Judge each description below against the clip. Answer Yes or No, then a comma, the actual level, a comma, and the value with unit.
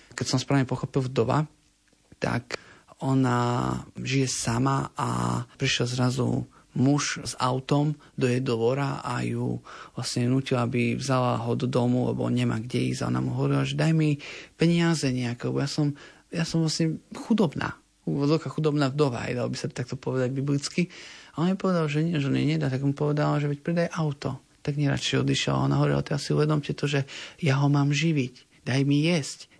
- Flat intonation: No, average, 3.2 semitones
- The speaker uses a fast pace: Yes, fast, 185 wpm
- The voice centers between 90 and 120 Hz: No, low, 135 Hz